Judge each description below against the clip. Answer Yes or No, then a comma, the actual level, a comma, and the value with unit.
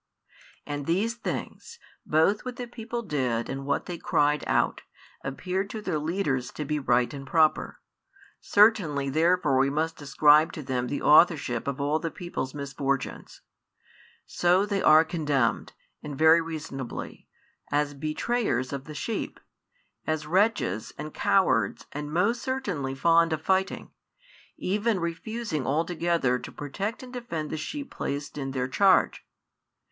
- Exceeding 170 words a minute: No, average, 145 wpm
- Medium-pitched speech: Yes, medium, 155 Hz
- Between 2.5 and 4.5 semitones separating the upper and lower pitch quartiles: No, average, 5.3 semitones